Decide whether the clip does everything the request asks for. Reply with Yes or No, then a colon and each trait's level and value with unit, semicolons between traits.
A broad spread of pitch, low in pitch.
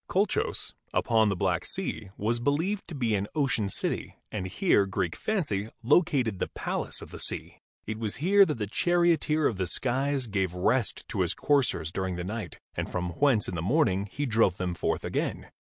Yes: wide, 7.1 semitones; low, 115 Hz